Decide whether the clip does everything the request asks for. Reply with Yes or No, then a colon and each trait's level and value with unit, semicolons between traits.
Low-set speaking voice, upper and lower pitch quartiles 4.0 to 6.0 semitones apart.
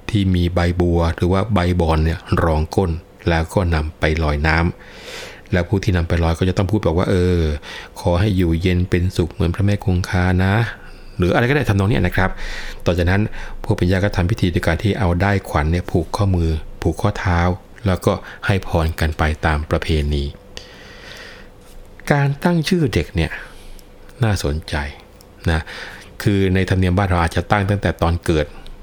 No: very low, 90 Hz; average, 3.2 semitones